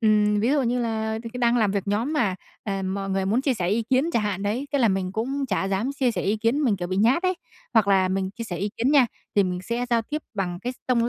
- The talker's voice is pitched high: Yes, high, 220 Hz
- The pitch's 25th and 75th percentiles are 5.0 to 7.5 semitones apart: No, average, 4.1 semitones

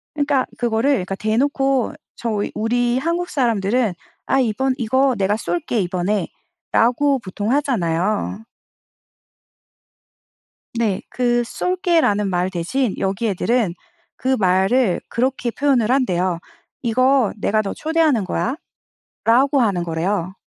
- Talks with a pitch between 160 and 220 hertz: No, high, 230 Hz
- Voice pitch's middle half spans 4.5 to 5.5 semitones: Yes, average, 5.2 semitones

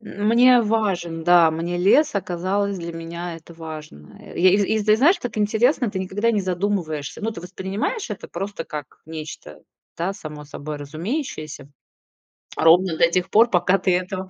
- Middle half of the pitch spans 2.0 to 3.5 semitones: No, average, 4.1 semitones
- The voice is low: No, medium, 185 Hz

